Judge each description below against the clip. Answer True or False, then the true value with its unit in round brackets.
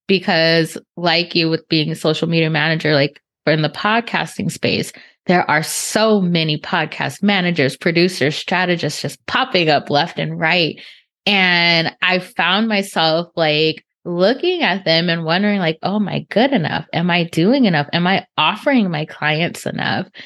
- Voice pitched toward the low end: False (170 Hz)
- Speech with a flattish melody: False (3.3 semitones)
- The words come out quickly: False (165 wpm)